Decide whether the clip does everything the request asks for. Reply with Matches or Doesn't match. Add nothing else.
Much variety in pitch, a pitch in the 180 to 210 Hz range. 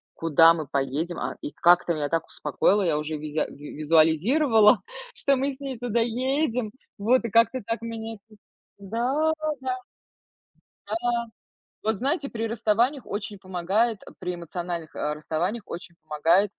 Matches